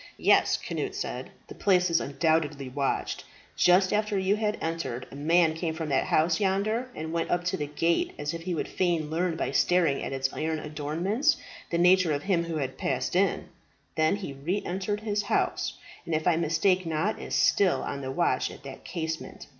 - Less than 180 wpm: No, average, 200 wpm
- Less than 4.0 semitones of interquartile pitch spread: Yes, average, 3.5 semitones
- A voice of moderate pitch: Yes, medium, 165 Hz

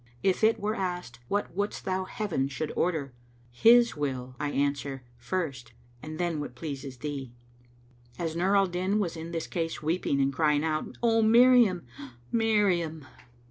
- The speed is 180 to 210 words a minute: No, average, 160 wpm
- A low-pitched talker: No, medium, 165 Hz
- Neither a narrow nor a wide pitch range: No, wide, 5.7 semitones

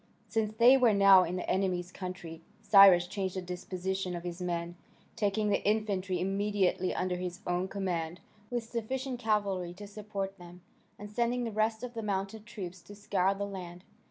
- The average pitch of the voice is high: Yes, high, 195 Hz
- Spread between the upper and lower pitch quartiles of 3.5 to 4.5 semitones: No, average, 2.8 semitones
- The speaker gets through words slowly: No, average, 175 wpm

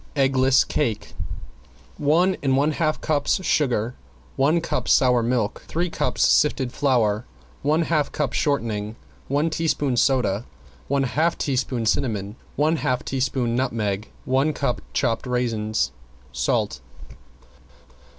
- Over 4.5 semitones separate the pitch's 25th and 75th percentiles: No, average, 4.2 semitones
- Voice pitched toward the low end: Yes, low, 130 Hz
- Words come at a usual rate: No, slow, 120 wpm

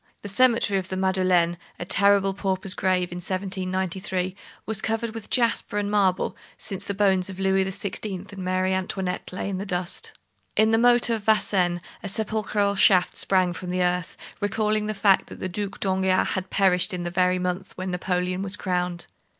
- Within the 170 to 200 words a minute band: Yes, average, 185 wpm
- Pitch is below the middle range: No, high, 190 Hz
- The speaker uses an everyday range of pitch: No, narrow, 1.7 semitones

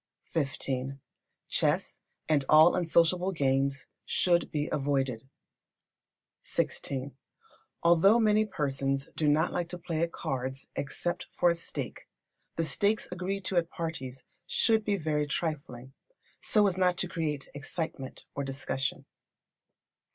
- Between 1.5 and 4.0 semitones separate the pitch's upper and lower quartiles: No, average, 4.5 semitones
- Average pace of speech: No, slow, 125 wpm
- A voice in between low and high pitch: Yes, medium, 155 Hz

